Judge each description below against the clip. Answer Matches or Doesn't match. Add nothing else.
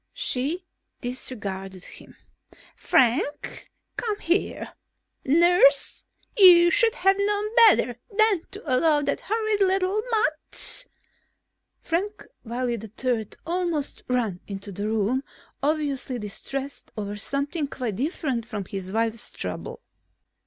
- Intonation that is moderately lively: Doesn't match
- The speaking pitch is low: Doesn't match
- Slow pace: Matches